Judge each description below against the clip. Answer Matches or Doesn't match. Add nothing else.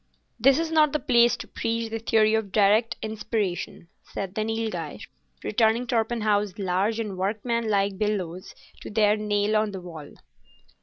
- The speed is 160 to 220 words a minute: Doesn't match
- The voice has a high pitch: Matches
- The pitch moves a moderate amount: Doesn't match